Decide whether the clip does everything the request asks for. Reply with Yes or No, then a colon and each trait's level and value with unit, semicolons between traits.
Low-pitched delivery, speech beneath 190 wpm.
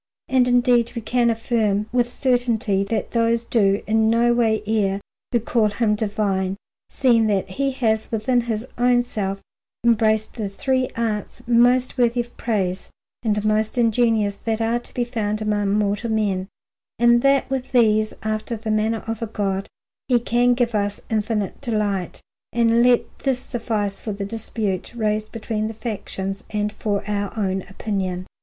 No: high, 220 Hz; average, 165 wpm